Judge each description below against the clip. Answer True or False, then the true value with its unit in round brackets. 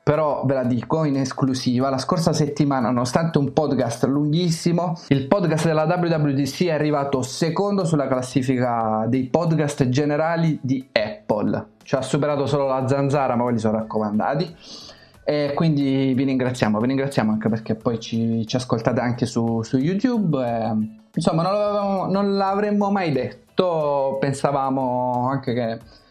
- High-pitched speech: False (135 Hz)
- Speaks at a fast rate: False (150 wpm)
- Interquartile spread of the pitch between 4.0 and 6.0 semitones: True (4.3 semitones)